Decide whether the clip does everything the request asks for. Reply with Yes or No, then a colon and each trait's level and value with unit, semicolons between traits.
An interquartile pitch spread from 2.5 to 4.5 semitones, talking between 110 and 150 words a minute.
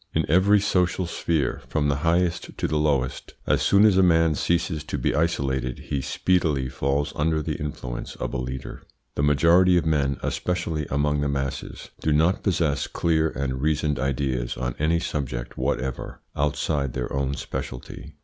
No: average, 3.5 semitones; average, 170 wpm